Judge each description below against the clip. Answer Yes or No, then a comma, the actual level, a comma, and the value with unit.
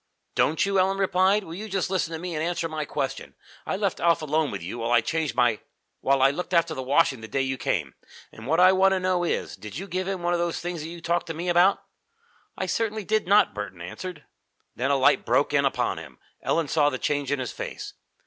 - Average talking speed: No, fast, 245 wpm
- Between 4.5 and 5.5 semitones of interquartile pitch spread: Yes, average, 5.1 semitones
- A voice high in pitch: No, medium, 165 Hz